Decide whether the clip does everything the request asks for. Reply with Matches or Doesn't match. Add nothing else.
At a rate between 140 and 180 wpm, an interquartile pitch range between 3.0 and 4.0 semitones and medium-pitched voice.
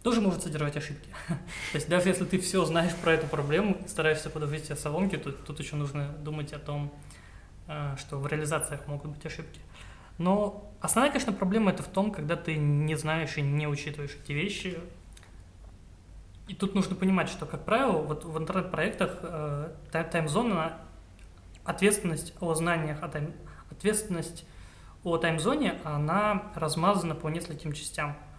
Matches